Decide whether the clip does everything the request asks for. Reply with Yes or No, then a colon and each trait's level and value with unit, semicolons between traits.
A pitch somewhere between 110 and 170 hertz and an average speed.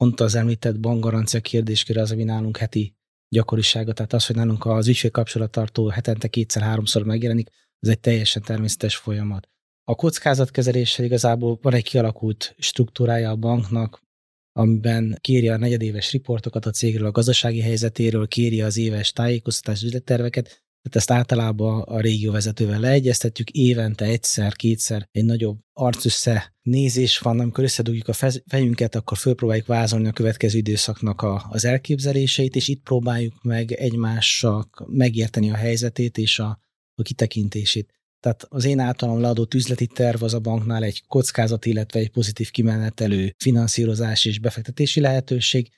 Yes: low, 115 Hz; average, 140 wpm